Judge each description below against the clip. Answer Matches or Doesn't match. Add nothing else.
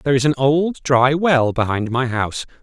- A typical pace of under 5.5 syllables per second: Matches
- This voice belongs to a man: Matches